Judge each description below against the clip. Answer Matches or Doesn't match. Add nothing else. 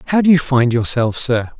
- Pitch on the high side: Doesn't match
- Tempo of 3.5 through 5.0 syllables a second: Doesn't match